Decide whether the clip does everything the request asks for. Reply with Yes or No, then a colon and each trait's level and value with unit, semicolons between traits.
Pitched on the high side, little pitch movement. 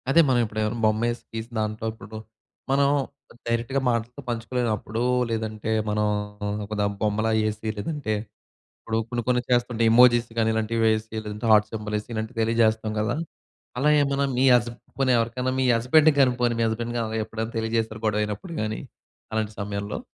No: low, 115 Hz; narrow, 1.9 semitones